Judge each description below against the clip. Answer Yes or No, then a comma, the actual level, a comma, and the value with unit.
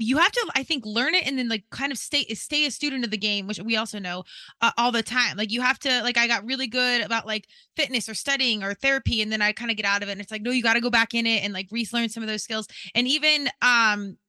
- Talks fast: Yes, fast, 305 wpm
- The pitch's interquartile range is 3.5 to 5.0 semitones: No, average, 3.1 semitones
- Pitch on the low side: No, high, 230 Hz